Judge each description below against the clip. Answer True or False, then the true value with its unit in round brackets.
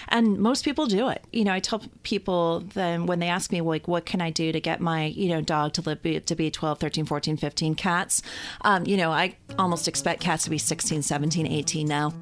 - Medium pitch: True (165 Hz)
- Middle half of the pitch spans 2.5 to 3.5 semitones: True (2.9 semitones)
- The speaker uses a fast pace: True (235 wpm)